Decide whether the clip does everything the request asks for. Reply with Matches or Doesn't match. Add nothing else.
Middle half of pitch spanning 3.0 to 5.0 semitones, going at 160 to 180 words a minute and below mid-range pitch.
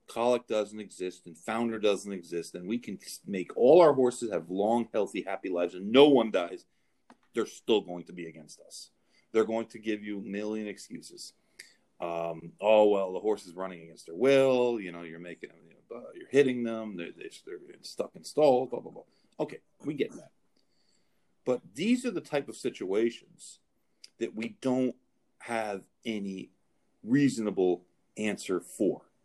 Matches